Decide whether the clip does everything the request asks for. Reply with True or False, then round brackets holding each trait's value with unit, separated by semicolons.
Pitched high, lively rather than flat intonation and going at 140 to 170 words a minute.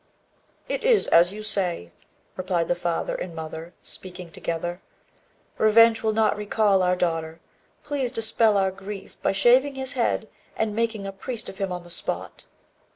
False (195 Hz; 4.1 semitones; 160 wpm)